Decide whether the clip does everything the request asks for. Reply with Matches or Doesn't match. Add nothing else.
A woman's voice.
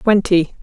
Matches